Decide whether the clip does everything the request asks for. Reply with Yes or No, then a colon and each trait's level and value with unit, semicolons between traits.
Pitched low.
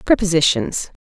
No: medium, 175 Hz